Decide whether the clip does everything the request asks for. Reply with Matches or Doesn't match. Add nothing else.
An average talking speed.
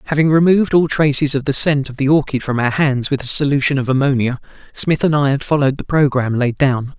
Doesn't match